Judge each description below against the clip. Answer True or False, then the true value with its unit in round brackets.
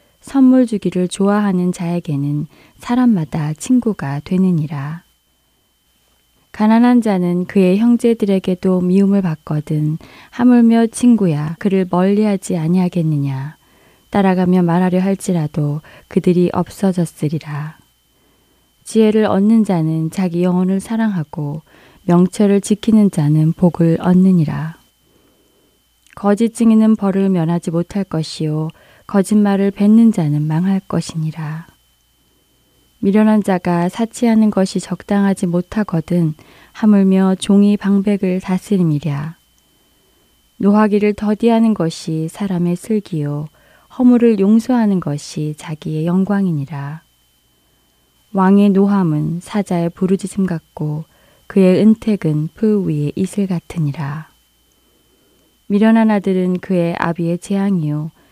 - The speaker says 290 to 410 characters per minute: False (255 characters per minute)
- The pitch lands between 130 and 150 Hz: False (180 Hz)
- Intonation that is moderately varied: True (4.3 semitones)